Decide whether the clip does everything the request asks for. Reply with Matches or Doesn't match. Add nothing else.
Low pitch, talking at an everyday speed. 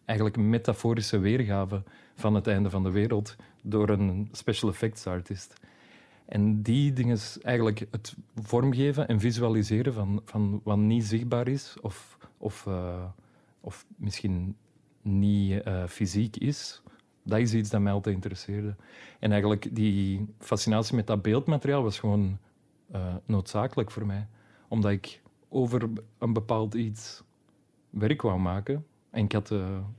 Matches